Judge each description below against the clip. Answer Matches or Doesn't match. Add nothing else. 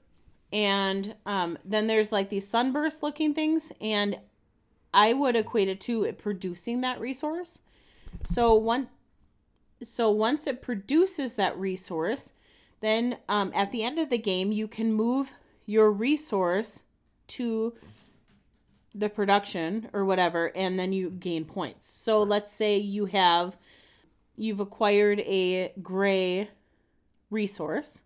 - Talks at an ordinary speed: Doesn't match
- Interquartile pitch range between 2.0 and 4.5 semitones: Matches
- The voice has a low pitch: Doesn't match